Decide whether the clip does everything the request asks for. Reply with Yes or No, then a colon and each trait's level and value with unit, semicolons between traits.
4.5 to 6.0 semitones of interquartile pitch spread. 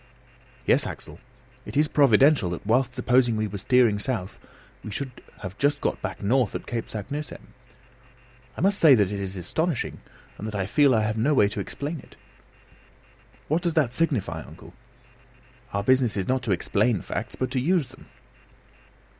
Yes: wide, 5.5 semitones